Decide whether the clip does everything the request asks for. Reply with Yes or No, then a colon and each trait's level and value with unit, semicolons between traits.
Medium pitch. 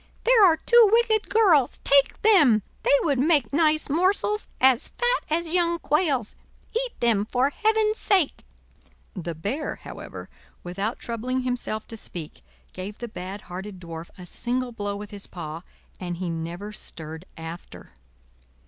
No: high, 245 Hz